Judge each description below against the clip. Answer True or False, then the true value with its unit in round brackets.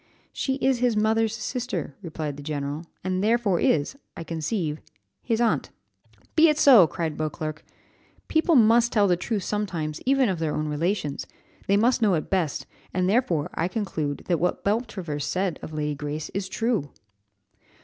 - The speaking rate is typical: True (165 wpm)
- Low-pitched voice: False (185 Hz)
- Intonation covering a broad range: True (6.6 semitones)